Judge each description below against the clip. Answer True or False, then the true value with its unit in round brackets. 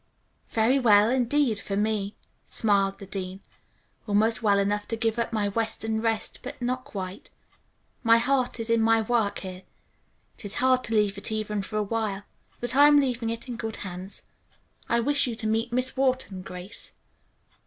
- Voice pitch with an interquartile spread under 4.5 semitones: True (2.8 semitones)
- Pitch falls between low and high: False (225 Hz)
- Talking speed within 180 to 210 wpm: True (185 wpm)